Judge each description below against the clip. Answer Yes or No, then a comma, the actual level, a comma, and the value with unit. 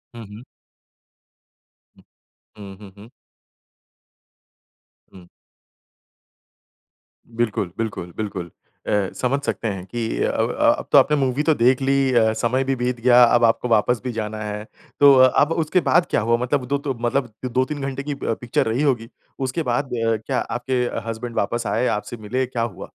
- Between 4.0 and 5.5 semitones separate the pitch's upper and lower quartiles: No, average, 3.2 semitones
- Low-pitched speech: Yes, low, 120 Hz